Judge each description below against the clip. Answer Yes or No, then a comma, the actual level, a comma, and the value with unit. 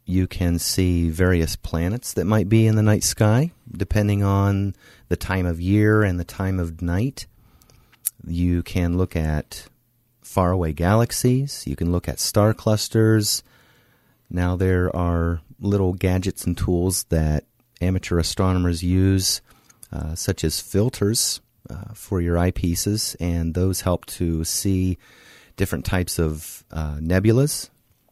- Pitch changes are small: No, average, 3.7 semitones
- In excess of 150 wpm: No, slow, 135 wpm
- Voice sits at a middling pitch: No, very low, 95 Hz